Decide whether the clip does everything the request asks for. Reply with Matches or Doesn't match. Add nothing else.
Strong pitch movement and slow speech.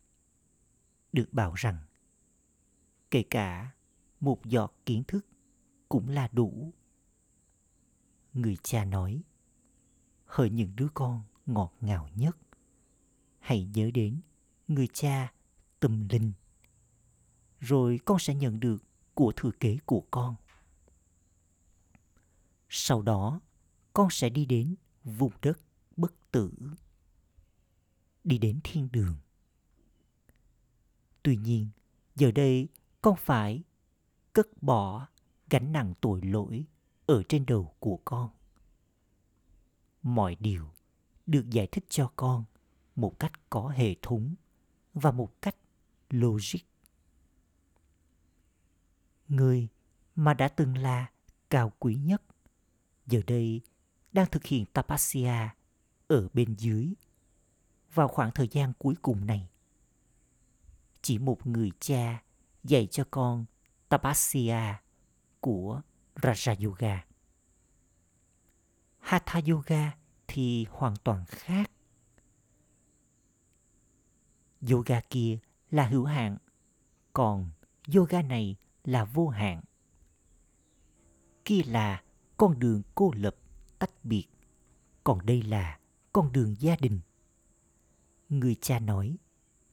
Matches